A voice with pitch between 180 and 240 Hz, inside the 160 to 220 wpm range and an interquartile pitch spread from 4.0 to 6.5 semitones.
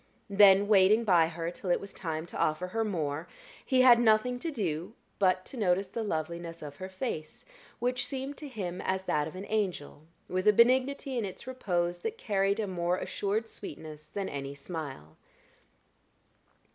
Yes: high, 190 Hz; average, 175 wpm; average, 4.9 semitones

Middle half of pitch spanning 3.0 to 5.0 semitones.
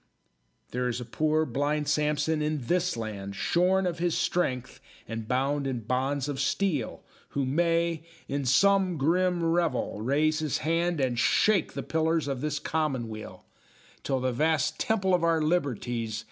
Yes: average, 4.5 semitones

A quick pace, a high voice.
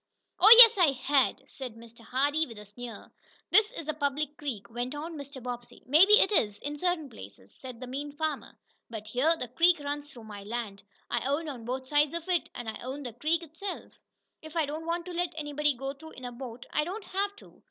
Yes: fast, 225 wpm; very high, 285 Hz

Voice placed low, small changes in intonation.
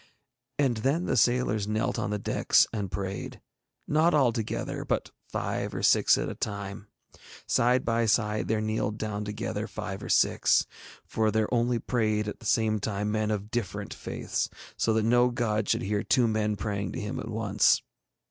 Yes: low, 110 Hz; narrow, 2.0 semitones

